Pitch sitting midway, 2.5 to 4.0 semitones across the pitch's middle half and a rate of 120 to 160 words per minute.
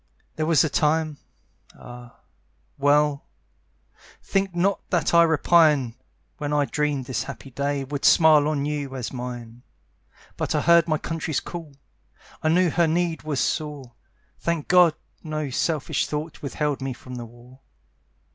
Yes: medium, 150 Hz; average, 3.0 semitones; average, 145 wpm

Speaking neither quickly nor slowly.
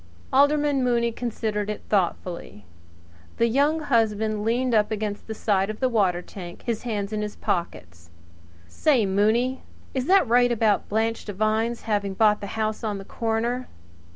Yes: average, 155 wpm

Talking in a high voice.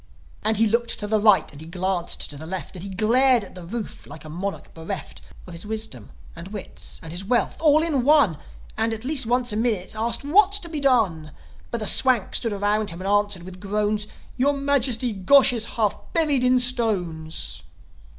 Yes: high, 215 Hz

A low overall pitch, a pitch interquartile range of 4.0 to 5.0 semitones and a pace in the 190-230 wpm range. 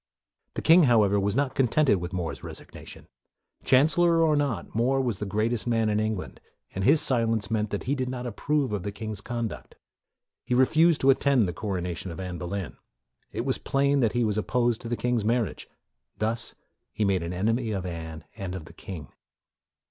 Yes: low, 110 Hz; average, 4.7 semitones; average, 200 wpm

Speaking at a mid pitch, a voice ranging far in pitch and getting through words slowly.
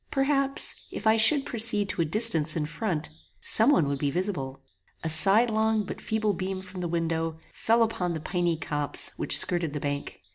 No: medium, 180 Hz; wide, 5.7 semitones; average, 185 wpm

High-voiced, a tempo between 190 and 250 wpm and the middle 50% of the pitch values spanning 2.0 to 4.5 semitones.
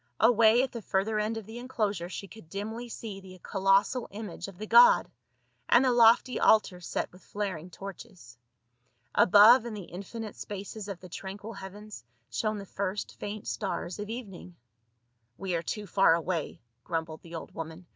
No: high, 200 Hz; average, 170 wpm; average, 3.3 semitones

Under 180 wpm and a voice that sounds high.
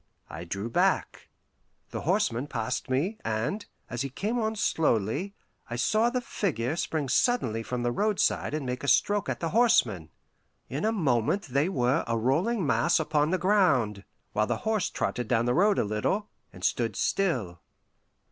No: average, 170 wpm; medium, 140 Hz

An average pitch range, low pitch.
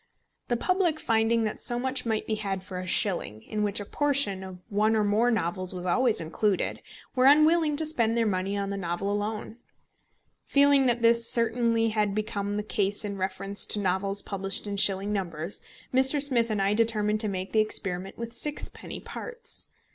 No: average, 3.2 semitones; high, 215 Hz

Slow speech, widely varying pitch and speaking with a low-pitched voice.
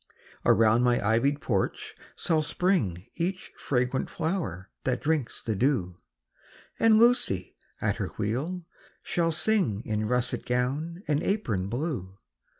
Yes: slow, 125 wpm; wide, 7.5 semitones; low, 130 Hz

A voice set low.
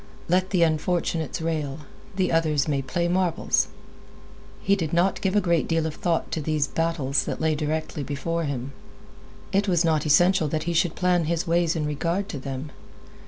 No: medium, 165 Hz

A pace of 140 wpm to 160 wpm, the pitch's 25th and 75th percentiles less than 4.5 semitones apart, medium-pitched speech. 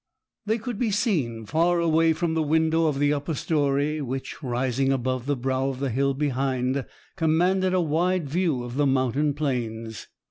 No: average, 175 wpm; average, 3.8 semitones; medium, 145 Hz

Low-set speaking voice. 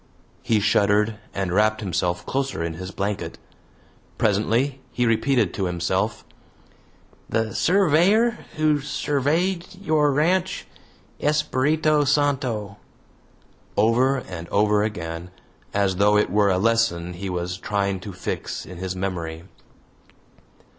Yes: low, 105 Hz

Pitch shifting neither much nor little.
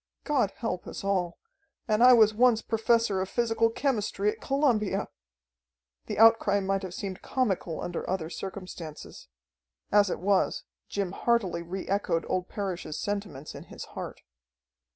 Yes: average, 3.4 semitones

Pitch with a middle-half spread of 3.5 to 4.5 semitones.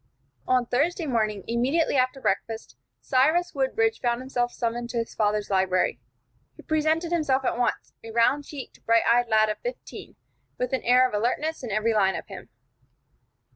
Yes: average, 3.8 semitones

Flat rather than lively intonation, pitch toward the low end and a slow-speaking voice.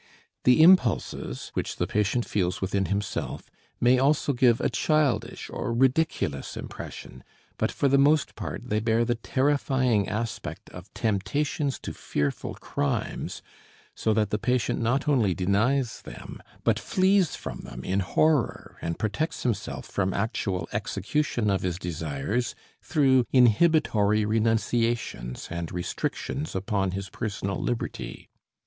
No: average, 5.3 semitones; low, 115 Hz; slow, 130 wpm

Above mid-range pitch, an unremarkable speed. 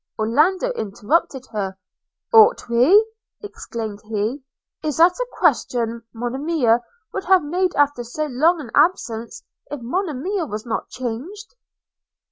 No: very high, 280 Hz; slow, 125 wpm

